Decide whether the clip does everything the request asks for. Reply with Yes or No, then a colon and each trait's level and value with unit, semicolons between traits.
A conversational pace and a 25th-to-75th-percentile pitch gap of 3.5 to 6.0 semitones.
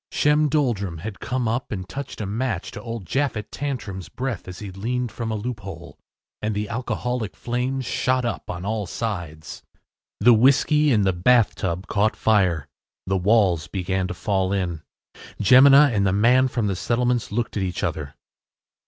Yes: average, 170 wpm; average, 4.7 semitones